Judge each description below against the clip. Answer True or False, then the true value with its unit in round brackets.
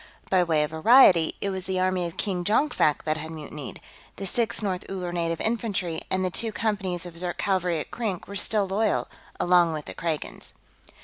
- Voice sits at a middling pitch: True (180 Hz)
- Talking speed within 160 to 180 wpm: False (195 wpm)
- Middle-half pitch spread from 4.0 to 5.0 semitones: False (3.1 semitones)